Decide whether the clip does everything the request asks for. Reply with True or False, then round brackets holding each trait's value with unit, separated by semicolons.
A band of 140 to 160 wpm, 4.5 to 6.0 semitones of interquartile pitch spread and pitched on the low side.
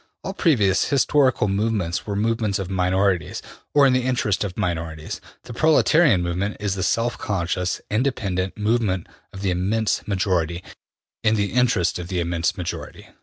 False (155 wpm; 4.1 semitones; 100 Hz)